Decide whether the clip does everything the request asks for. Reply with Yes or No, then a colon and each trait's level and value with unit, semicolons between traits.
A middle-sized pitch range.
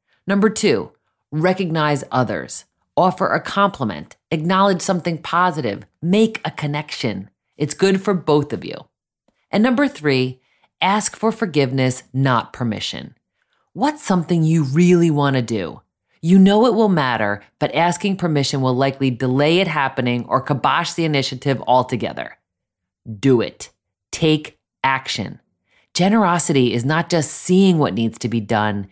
No: wide, 6.3 semitones